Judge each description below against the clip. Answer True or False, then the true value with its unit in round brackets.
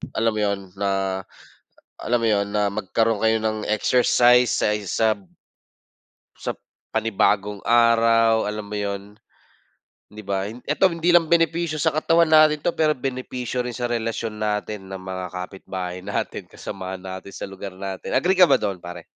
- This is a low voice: True (110 Hz)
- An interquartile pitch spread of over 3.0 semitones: True (3.8 semitones)